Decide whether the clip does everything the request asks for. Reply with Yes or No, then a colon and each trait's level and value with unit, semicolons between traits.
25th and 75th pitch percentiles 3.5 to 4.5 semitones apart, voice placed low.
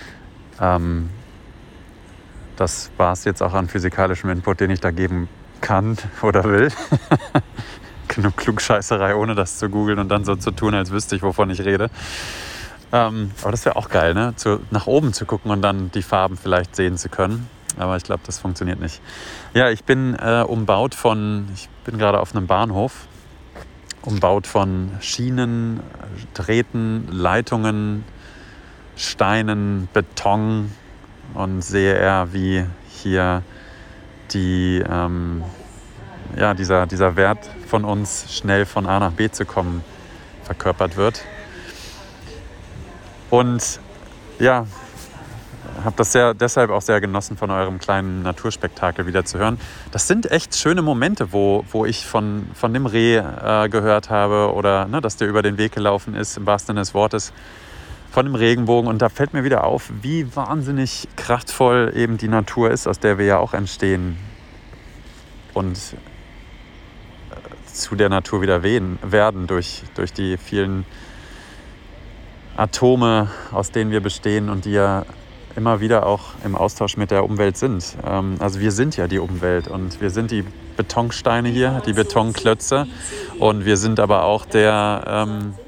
No: average, 2.9 semitones; low, 100 Hz